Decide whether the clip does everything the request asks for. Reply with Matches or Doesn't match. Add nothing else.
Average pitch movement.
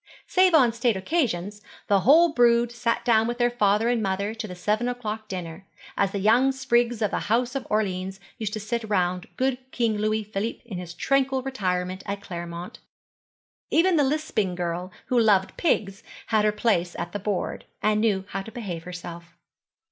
Matches